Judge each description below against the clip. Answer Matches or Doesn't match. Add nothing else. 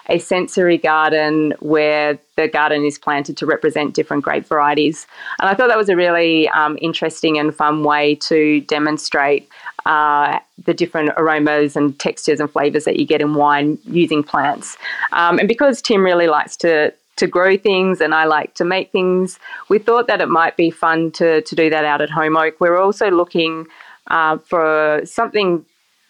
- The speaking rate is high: Doesn't match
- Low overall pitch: Doesn't match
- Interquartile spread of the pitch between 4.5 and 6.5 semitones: Doesn't match